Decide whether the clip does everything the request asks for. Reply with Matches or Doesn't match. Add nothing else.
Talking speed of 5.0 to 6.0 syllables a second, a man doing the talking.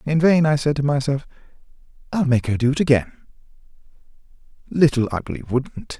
Matches